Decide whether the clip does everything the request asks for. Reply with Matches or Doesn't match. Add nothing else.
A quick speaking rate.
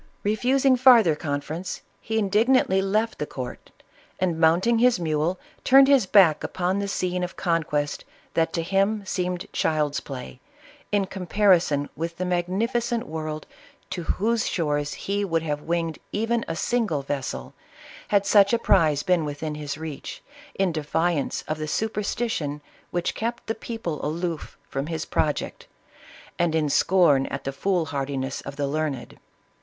Doesn't match